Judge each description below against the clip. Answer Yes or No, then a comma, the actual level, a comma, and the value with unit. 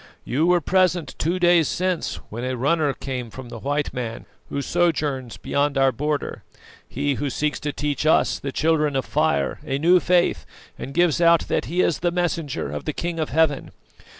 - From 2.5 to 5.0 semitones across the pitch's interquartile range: Yes, average, 4.0 semitones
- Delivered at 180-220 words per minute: Yes, average, 190 wpm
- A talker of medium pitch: Yes, medium, 150 Hz